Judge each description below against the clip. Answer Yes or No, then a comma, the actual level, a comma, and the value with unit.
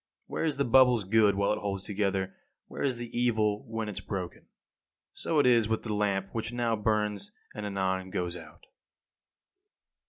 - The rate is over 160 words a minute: Yes, average, 180 wpm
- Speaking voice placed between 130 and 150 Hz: No, low, 105 Hz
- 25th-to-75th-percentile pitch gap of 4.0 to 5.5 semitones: No, average, 3.1 semitones